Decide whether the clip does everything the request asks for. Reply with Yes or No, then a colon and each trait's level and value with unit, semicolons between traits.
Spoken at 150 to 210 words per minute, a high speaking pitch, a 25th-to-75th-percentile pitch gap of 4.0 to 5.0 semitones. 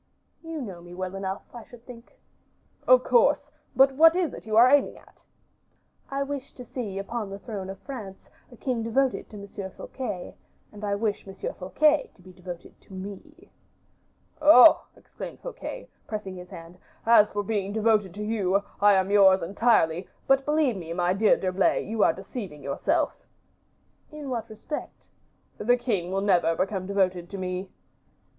Yes: average, 170 wpm; high, 205 Hz; average, 4.6 semitones